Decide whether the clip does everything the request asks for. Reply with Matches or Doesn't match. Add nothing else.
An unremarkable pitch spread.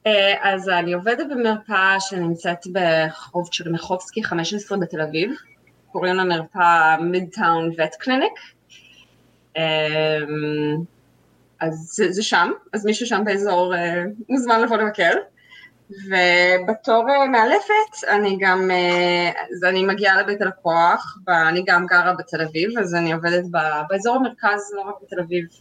Matches